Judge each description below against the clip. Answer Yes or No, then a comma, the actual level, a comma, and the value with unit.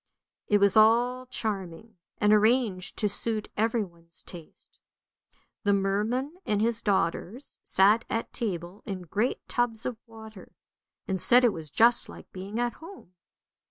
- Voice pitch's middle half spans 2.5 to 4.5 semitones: Yes, average, 3.4 semitones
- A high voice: Yes, high, 215 Hz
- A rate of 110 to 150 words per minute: Yes, average, 140 wpm